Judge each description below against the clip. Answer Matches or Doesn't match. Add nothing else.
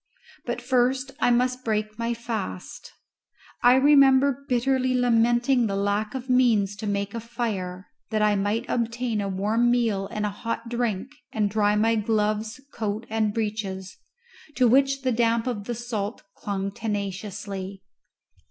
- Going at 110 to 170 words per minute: Matches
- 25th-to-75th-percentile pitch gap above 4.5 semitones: Doesn't match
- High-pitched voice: Matches